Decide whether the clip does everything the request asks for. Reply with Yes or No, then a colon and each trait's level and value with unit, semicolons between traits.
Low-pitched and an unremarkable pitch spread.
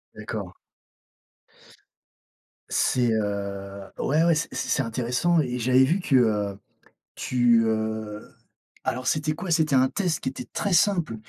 No: low, 125 Hz; wide, 6.0 semitones